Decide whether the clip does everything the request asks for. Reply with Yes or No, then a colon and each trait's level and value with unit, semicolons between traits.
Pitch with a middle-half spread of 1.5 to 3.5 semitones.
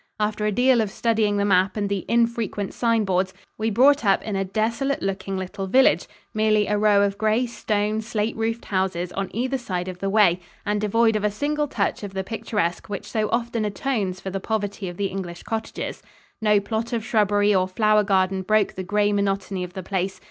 Yes: narrow, 2.4 semitones